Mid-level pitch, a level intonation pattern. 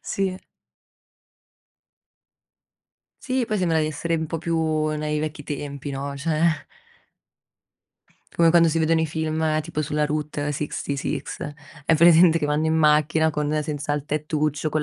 Yes: medium, 155 Hz; narrow, 1.6 semitones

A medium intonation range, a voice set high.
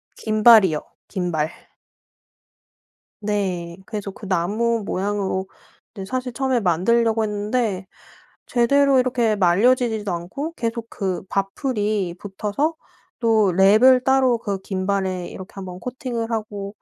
Yes: average, 3.7 semitones; high, 210 Hz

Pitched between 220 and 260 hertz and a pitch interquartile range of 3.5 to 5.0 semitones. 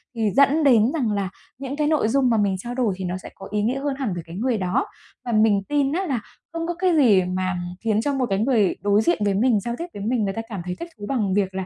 No: high, 225 Hz; wide, 5.5 semitones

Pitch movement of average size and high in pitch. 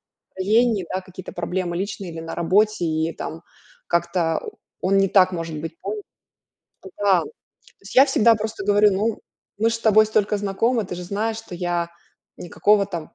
Yes: average, 3.7 semitones; high, 195 Hz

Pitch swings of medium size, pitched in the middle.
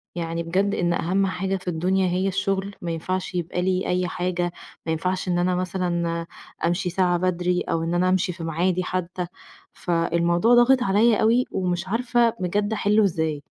No: narrow, 1.9 semitones; medium, 180 Hz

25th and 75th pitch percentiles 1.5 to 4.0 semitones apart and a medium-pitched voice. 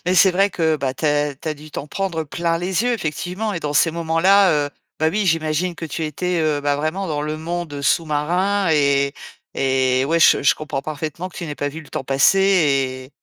Yes: average, 3.5 semitones; medium, 160 Hz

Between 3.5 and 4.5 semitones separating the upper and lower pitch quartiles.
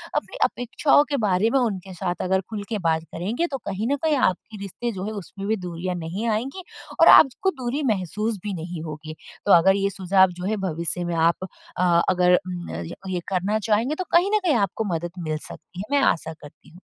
Yes: average, 4.2 semitones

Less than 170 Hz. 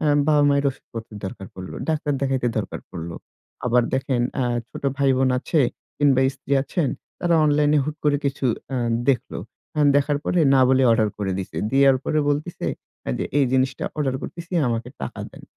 Yes: low, 135 Hz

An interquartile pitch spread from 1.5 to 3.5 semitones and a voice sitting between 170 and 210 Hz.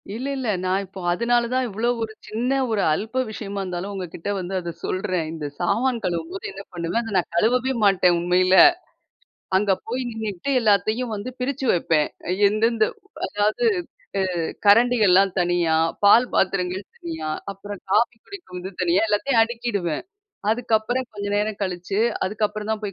No: average, 4.0 semitones; high, 205 Hz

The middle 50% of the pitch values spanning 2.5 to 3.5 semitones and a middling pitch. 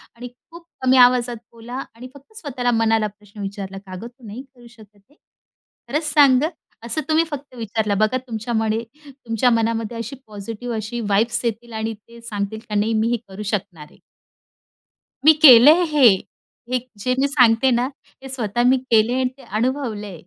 No: average, 3.1 semitones; high, 235 Hz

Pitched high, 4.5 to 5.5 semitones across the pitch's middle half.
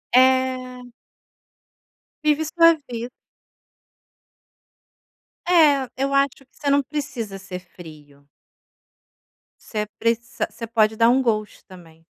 Yes: high, 240 Hz; average, 4.9 semitones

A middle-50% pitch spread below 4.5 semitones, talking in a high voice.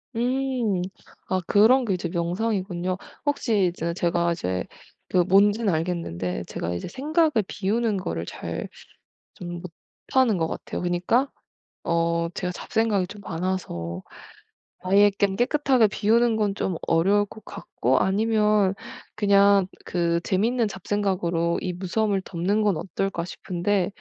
Yes: average, 3.8 semitones; high, 195 Hz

